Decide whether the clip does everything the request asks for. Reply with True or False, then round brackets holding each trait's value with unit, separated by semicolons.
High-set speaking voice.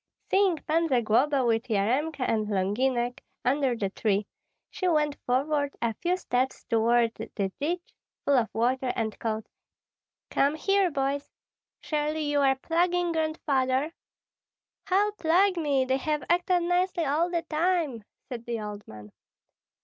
True (280 Hz)